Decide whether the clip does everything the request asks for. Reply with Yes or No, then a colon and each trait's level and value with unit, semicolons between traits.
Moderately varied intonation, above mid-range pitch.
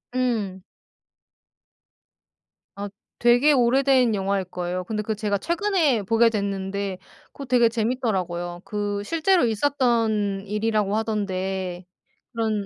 Yes: average, 3.6 semitones; high, 215 Hz